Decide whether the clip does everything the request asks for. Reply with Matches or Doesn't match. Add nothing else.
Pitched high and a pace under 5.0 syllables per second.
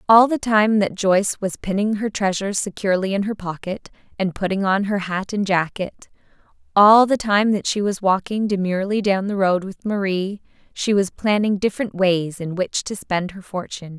Doesn't match